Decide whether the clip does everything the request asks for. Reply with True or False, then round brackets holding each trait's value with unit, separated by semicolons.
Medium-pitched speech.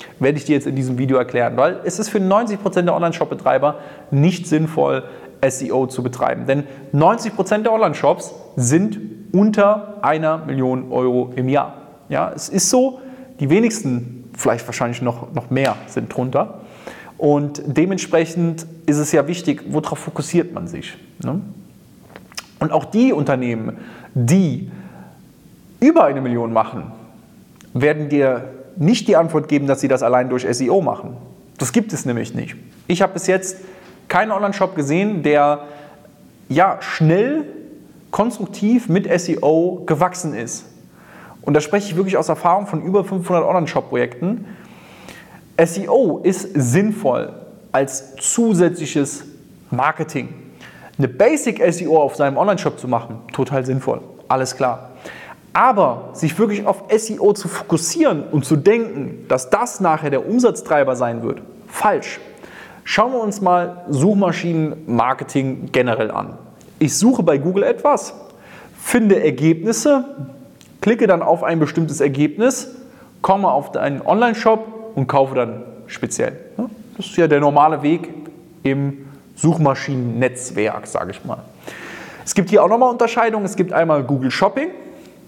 True (160 Hz)